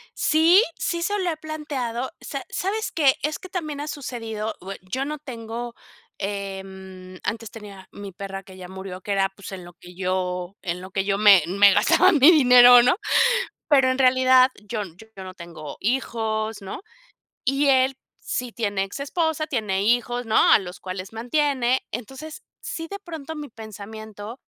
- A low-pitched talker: No, high, 225 Hz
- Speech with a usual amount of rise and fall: No, wide, 6.1 semitones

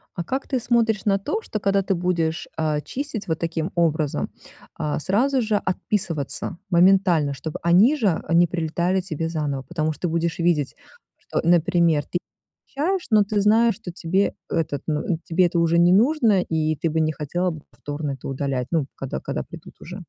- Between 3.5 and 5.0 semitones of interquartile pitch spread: Yes, average, 4.1 semitones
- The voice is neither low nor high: Yes, medium, 170 Hz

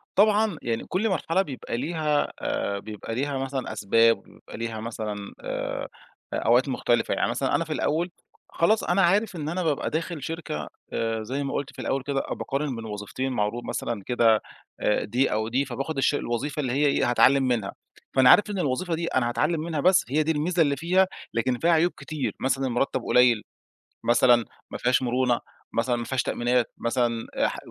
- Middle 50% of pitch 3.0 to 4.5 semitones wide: No, wide, 5.4 semitones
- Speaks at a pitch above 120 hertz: Yes, low, 135 Hz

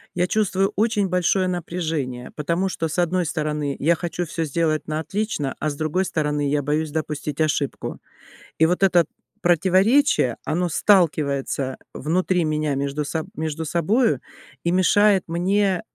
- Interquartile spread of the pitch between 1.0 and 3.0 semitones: No, average, 3.5 semitones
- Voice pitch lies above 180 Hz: No, medium, 165 Hz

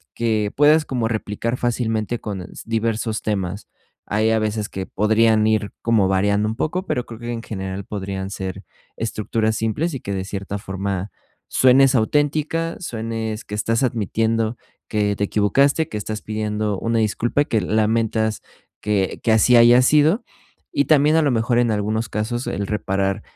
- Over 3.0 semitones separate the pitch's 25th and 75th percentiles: No, narrow, 2.5 semitones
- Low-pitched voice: Yes, low, 110 Hz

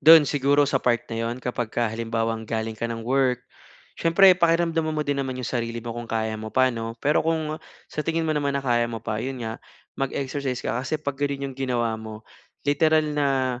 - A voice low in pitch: Yes, low, 130 Hz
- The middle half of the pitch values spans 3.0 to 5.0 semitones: Yes, average, 4.0 semitones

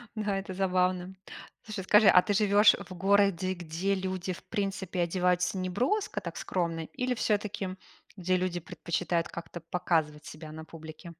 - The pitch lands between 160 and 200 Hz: Yes, medium, 185 Hz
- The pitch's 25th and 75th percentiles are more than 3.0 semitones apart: No, narrow, 2.4 semitones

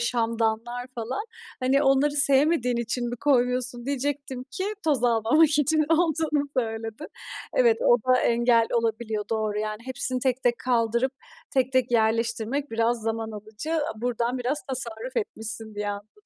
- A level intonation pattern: No, average, 3.2 semitones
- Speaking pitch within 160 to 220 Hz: No, high, 245 Hz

